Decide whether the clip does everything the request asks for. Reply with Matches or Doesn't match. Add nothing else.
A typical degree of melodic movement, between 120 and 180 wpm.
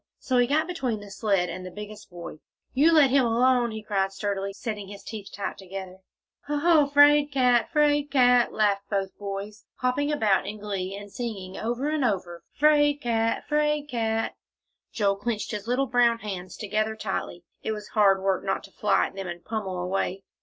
Doesn't match